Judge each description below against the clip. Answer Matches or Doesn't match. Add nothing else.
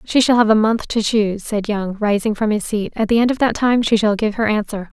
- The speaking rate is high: Matches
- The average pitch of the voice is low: Doesn't match